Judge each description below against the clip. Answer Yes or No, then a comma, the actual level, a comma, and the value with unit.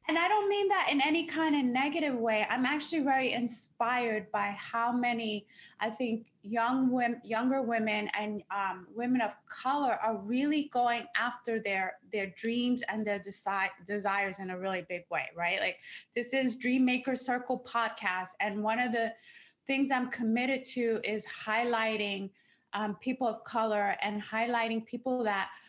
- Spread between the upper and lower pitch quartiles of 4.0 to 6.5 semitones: No, average, 3.5 semitones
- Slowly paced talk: No, average, 165 wpm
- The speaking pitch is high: Yes, high, 230 Hz